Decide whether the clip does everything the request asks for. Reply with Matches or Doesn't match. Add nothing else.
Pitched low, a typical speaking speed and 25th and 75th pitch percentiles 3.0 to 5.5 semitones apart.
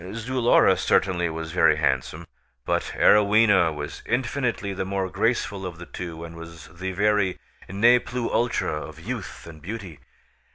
Matches